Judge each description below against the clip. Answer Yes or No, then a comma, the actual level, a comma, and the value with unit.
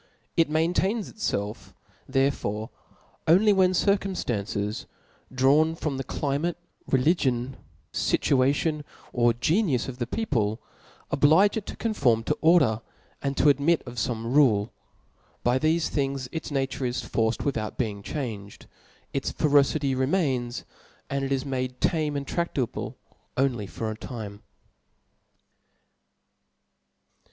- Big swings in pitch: No, average, 4.7 semitones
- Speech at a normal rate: No, slow, 125 wpm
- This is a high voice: No, low, 135 Hz